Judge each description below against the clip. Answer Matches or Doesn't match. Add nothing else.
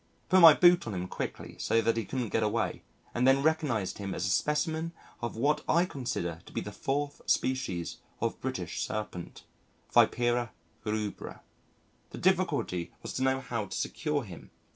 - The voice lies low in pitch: Matches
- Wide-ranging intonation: Matches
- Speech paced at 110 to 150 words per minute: Doesn't match